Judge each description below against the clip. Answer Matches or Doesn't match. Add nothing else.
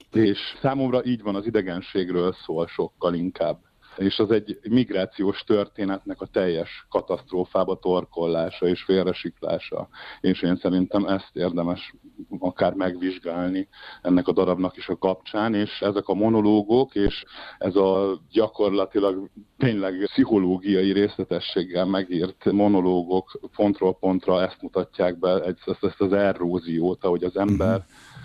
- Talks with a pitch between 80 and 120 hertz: Matches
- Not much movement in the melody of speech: Matches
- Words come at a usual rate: Matches